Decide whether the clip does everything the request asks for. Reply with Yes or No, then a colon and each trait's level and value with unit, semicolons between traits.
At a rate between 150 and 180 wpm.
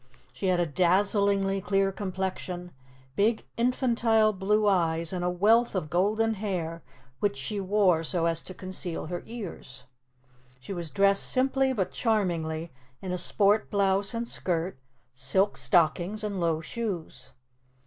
No: average, 140 wpm